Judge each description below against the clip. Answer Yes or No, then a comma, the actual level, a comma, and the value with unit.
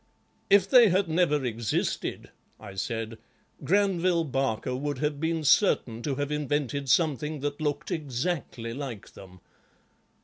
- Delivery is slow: Yes, slow, 130 wpm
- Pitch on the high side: No, medium, 145 Hz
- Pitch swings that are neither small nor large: Yes, average, 4.8 semitones